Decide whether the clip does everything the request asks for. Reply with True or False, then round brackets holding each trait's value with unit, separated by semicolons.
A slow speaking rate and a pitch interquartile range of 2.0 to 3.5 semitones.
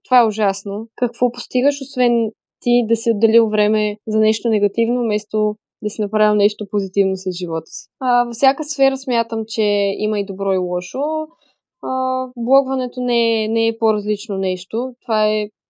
False (165 wpm; 2.7 semitones)